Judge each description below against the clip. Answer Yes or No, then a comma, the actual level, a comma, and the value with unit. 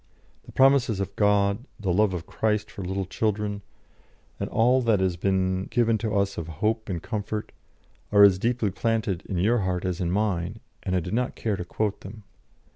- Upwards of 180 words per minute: Yes, average, 195 wpm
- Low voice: Yes, low, 100 Hz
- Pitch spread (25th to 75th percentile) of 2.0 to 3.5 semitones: Yes, average, 2.8 semitones